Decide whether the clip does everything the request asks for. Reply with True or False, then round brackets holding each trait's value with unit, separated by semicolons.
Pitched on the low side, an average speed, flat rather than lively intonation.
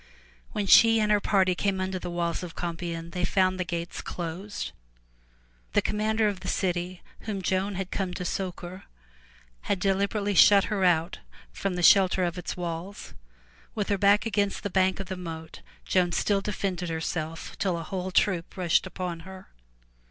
False (185 Hz; 175 wpm; 2.2 semitones)